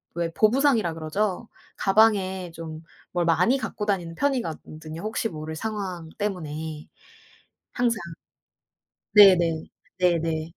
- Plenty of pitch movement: No, average, 4.8 semitones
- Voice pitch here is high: No, medium, 180 Hz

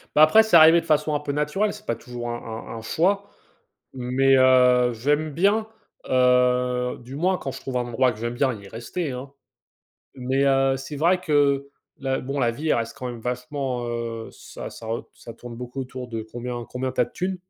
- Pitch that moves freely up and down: No, average, 3.3 semitones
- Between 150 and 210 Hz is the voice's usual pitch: No, low, 130 Hz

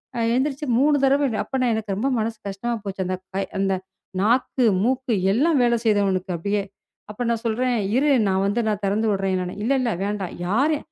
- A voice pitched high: Yes, high, 220 Hz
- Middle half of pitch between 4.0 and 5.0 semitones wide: Yes, average, 4.6 semitones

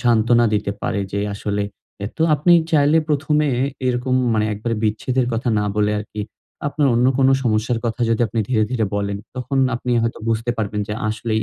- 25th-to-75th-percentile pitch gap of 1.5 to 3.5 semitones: Yes, average, 3.1 semitones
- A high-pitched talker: No, low, 115 Hz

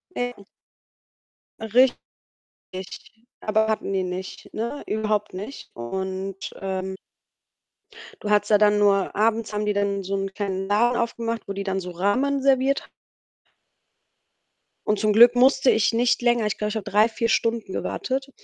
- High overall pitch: Yes, high, 210 Hz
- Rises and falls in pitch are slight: No, average, 3.2 semitones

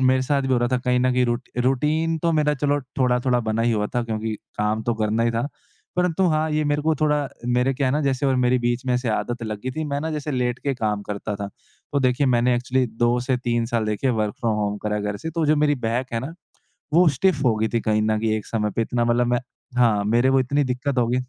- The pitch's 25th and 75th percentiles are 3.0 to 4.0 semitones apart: Yes, average, 3.5 semitones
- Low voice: Yes, low, 125 Hz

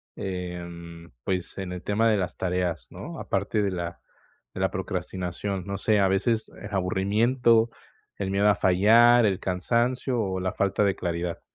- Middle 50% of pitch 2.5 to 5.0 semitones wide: Yes, average, 2.8 semitones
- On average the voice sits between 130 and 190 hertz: No, very low, 95 Hz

